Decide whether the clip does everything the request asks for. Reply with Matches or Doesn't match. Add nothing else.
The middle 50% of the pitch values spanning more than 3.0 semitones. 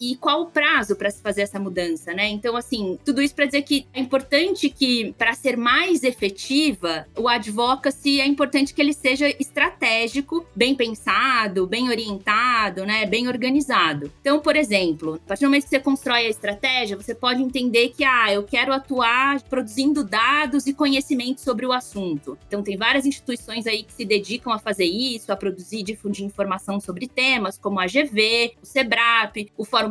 Matches